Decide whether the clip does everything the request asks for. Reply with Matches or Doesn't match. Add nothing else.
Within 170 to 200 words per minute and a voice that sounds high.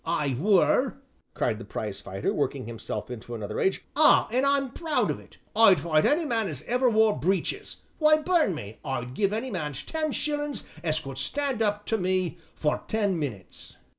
Matches